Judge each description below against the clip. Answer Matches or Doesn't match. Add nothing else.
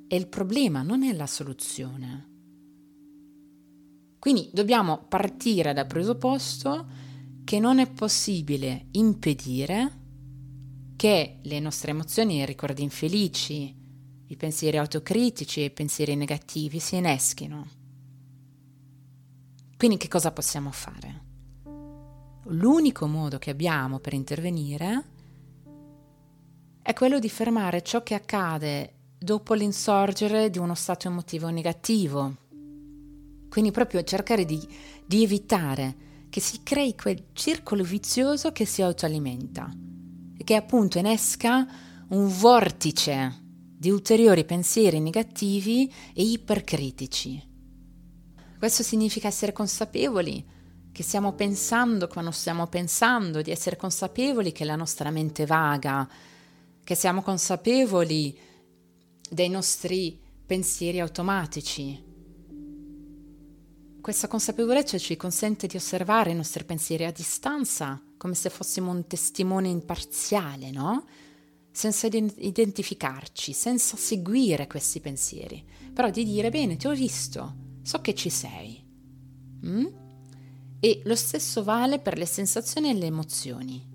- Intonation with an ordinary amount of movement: Doesn't match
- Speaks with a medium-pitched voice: Matches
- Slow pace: Matches